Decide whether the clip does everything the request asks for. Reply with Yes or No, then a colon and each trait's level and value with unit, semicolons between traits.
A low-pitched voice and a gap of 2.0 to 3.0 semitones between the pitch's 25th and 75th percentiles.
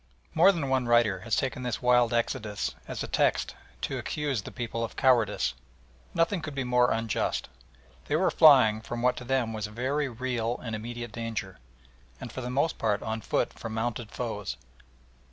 Yes: low, 120 Hz; narrow, 2.6 semitones